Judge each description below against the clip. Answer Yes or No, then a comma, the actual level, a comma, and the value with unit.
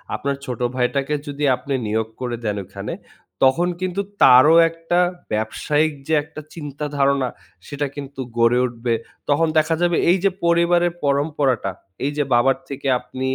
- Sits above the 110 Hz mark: Yes, medium, 140 Hz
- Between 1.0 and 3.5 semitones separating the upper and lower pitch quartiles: No, average, 4.3 semitones